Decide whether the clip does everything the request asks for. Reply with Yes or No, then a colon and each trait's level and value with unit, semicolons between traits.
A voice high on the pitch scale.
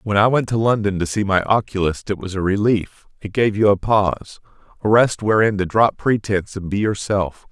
No: low, 105 Hz